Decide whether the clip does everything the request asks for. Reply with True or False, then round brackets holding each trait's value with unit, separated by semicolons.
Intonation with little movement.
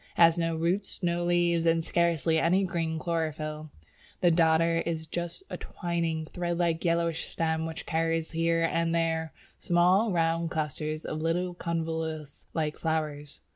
True (1.2 semitones)